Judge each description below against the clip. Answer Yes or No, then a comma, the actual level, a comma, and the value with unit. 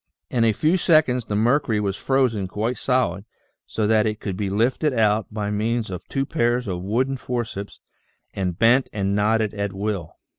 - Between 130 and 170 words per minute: No, average, 180 wpm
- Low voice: Yes, low, 110 Hz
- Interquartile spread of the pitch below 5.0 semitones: Yes, average, 3.5 semitones